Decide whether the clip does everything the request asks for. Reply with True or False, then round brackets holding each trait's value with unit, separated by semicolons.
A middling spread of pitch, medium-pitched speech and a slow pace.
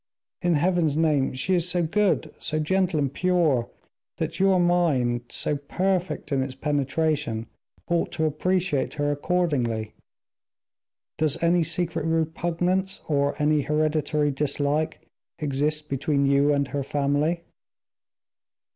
True (3.4 semitones; 155 Hz; 120 wpm)